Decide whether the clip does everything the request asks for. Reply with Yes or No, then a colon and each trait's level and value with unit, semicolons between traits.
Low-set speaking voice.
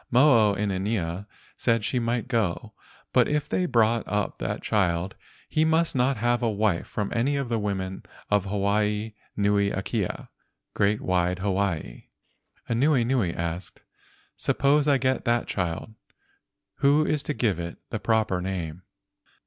Yes: low, 105 Hz